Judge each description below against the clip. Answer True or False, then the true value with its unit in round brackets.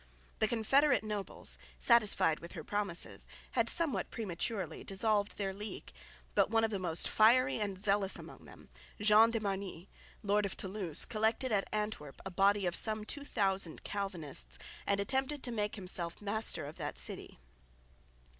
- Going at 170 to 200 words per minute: False (155 wpm)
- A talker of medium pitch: False (205 Hz)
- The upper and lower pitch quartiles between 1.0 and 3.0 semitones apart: True (2.6 semitones)